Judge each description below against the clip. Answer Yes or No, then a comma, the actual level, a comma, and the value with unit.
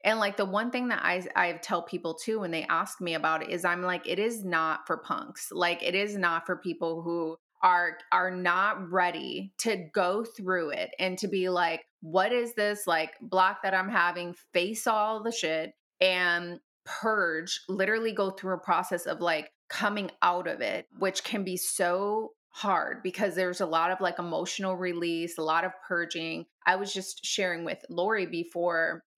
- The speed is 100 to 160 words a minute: No, average, 190 wpm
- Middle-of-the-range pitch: Yes, medium, 180 Hz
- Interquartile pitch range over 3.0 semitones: No, average, 2.7 semitones